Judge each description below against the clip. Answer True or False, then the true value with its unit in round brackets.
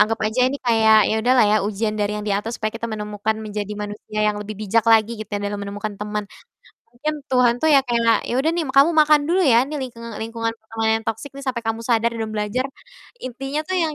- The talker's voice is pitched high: True (225 Hz)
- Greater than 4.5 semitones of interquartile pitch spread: False (3.2 semitones)